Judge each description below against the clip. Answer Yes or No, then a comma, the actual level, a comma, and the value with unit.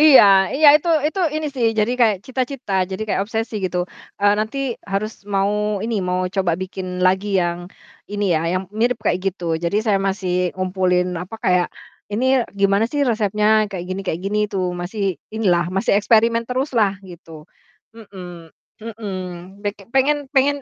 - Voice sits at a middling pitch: No, high, 205 Hz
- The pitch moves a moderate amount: Yes, average, 3.7 semitones